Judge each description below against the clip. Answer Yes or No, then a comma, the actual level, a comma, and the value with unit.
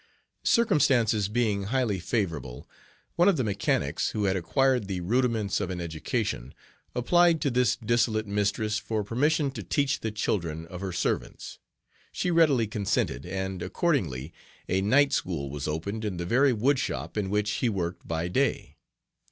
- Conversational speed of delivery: Yes, average, 155 wpm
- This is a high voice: No, low, 105 Hz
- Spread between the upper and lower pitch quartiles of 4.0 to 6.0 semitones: Yes, wide, 5.6 semitones